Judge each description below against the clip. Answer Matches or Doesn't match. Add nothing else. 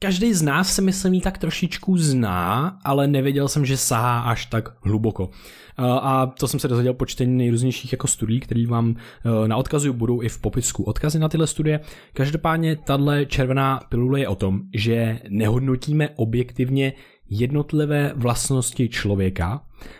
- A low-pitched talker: Matches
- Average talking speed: Matches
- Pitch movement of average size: Matches